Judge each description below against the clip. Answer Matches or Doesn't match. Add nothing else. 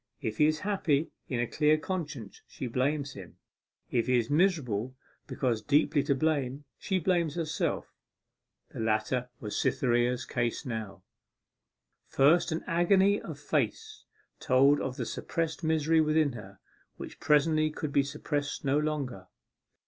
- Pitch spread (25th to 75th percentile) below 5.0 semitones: Matches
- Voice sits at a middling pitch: Matches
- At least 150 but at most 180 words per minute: Doesn't match